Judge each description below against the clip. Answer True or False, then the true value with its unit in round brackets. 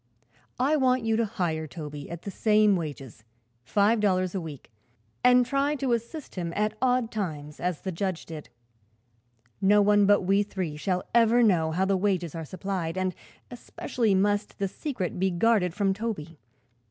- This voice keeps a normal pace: True (170 wpm)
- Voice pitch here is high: True (195 Hz)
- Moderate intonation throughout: True (4.6 semitones)